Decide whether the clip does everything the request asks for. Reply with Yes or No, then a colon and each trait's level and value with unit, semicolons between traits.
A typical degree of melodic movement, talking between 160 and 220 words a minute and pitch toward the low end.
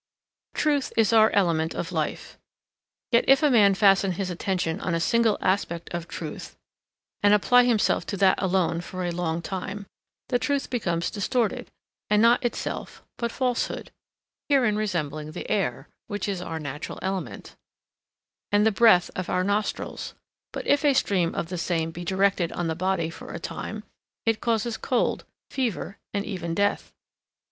No: average, 4.4 semitones; average, 165 wpm; high, 195 Hz